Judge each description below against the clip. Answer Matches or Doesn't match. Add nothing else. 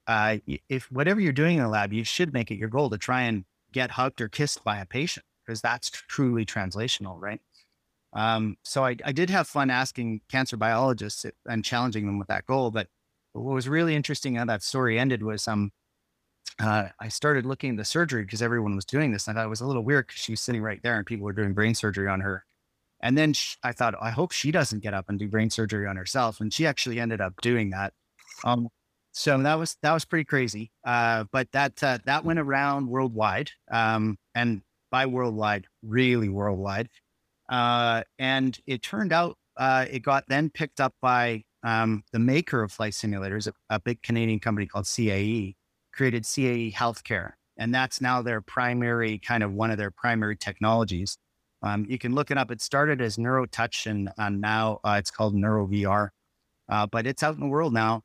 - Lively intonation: Doesn't match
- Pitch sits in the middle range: Doesn't match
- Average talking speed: Doesn't match